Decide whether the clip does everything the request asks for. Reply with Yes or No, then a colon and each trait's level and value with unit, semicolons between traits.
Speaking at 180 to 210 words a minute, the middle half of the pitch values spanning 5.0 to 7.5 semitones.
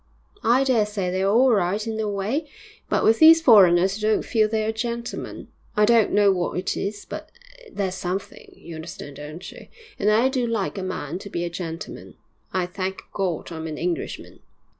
No: average, 190 wpm; average, 3.7 semitones